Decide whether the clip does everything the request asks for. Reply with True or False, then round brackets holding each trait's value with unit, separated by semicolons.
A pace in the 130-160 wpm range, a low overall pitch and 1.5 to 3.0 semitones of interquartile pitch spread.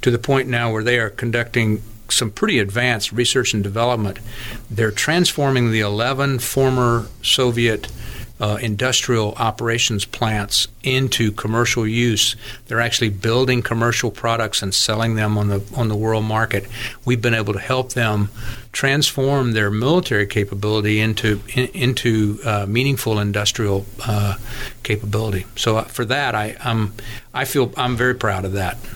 True (145 wpm; 115 Hz; 2.6 semitones)